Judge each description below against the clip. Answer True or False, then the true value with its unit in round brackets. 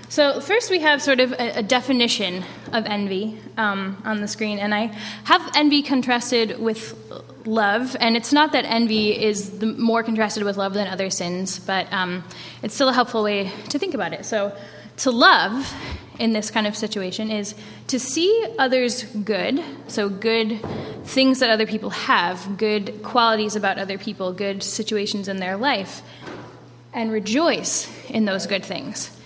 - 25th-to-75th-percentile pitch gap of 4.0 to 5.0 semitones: False (3.4 semitones)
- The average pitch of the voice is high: True (220 Hz)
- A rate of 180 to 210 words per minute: False (170 wpm)